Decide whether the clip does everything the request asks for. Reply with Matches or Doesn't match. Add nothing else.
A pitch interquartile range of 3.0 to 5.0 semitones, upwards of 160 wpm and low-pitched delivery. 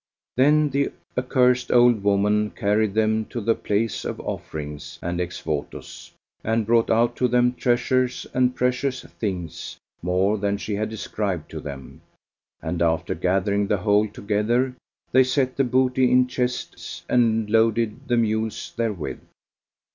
Doesn't match